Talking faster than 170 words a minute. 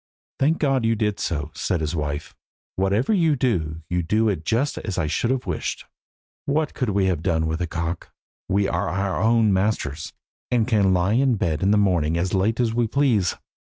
Yes: average, 200 wpm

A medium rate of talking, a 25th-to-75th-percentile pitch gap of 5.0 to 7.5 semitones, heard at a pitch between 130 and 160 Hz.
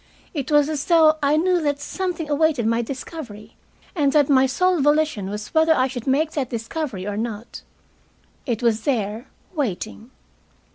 No: average, 160 wpm; average, 5.3 semitones; very high, 280 Hz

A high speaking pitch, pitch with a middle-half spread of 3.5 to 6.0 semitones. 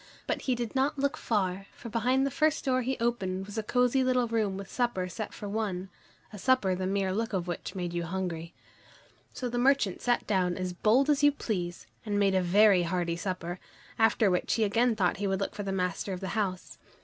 Yes: high, 205 Hz; average, 4.6 semitones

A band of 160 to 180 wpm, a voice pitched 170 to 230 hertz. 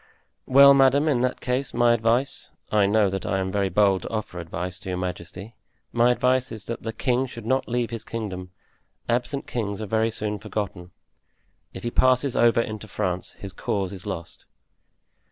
No: average, 175 wpm; low, 110 Hz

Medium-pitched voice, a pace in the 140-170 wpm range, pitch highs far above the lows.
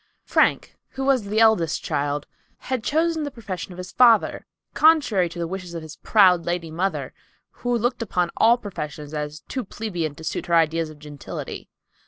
No: medium, 180 Hz; average, 180 wpm; wide, 6.4 semitones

